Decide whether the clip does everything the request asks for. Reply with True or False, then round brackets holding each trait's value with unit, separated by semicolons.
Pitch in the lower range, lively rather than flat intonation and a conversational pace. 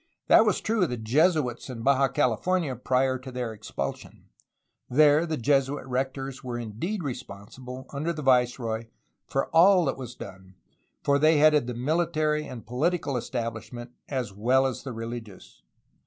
False (130 Hz; 4.1 semitones; 155 wpm)